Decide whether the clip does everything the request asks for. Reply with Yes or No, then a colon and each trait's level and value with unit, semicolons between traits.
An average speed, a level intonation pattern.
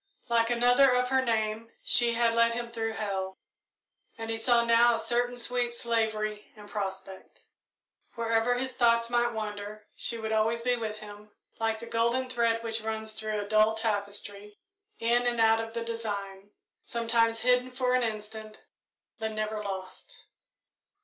Yes: average, 160 wpm; narrow, 1.7 semitones